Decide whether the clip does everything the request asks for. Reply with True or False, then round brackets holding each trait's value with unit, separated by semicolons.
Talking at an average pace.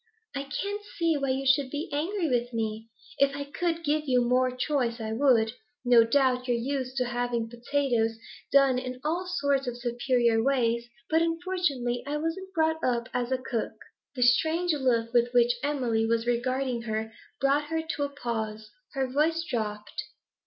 True (175 wpm)